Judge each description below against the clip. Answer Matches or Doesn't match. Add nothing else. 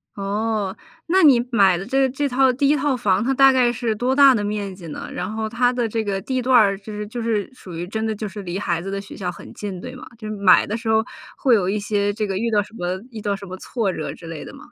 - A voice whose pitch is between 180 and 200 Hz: Doesn't match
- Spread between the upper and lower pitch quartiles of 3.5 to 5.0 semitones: Matches